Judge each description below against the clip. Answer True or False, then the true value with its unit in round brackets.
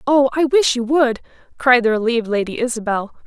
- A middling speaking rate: True (185 wpm)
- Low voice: False (245 Hz)